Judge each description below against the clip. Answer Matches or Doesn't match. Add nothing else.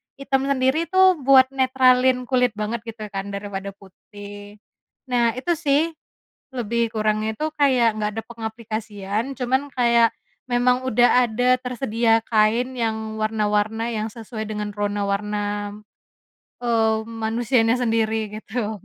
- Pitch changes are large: Doesn't match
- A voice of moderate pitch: Doesn't match